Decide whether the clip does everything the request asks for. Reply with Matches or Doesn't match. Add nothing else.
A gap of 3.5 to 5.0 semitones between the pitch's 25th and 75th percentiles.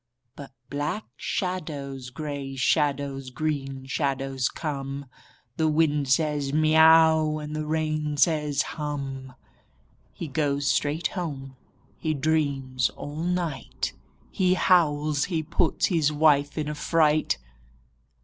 Doesn't match